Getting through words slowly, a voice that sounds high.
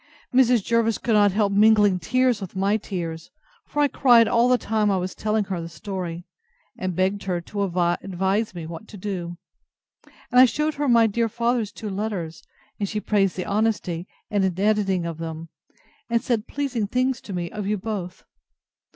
No: average, 185 wpm; high, 205 Hz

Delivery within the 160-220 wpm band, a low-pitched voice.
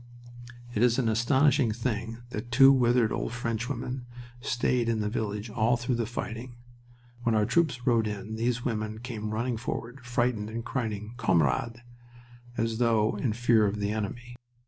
Yes: average, 165 wpm; low, 115 Hz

